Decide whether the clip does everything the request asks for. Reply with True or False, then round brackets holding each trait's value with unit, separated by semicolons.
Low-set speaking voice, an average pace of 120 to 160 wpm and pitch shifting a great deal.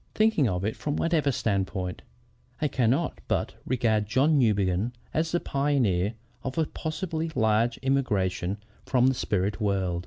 True (120 Hz; 145 wpm; 6.3 semitones)